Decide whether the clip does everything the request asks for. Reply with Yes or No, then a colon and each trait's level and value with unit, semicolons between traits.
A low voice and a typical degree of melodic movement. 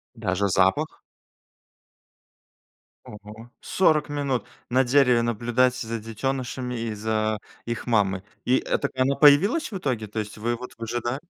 Yes: low, 120 Hz; average, 3.3 semitones